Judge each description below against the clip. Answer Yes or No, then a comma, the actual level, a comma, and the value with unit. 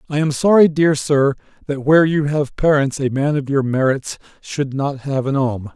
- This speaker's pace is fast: Yes, fast, 210 wpm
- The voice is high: No, medium, 140 Hz